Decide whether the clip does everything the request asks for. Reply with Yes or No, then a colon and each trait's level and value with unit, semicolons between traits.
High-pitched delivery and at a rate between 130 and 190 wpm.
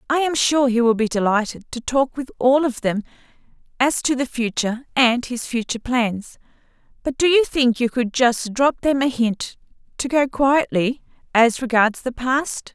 Yes: very high, 250 Hz; average, 185 wpm